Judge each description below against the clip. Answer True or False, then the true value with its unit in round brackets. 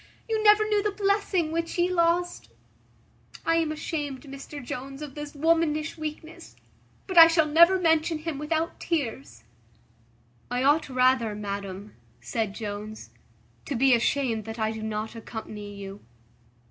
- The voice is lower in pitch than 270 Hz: False (295 Hz)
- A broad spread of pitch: True (6.8 semitones)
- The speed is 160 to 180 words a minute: False (145 wpm)